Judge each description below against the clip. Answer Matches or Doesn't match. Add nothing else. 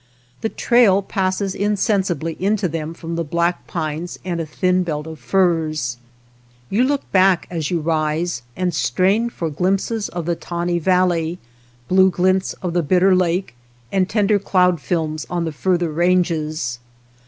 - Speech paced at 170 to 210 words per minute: Doesn't match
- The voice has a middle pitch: Matches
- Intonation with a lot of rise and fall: Doesn't match